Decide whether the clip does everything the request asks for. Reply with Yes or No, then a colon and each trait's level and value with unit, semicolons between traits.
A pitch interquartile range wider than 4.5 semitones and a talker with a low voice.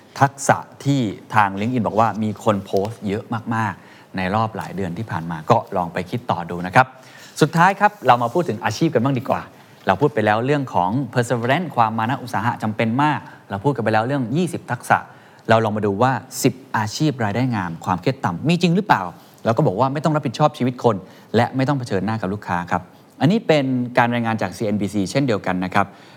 Yes: average, 5.1 semitones; low, 120 Hz